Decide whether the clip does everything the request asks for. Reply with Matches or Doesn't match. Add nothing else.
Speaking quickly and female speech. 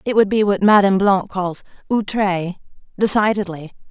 Doesn't match